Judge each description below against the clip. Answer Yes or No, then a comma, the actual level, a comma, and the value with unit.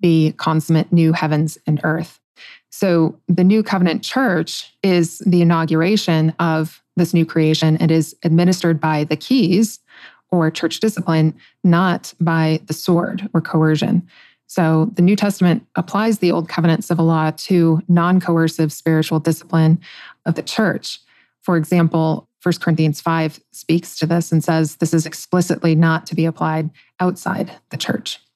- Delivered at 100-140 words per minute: No, average, 150 wpm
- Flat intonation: Yes, narrow, 2.1 semitones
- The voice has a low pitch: No, medium, 165 Hz